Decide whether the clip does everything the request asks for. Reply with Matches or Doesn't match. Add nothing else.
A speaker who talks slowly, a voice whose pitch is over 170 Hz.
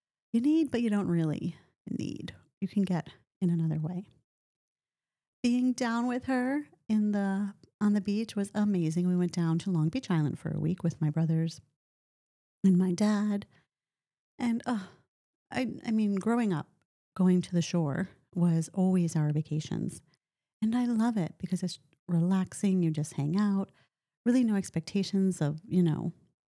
Doesn't match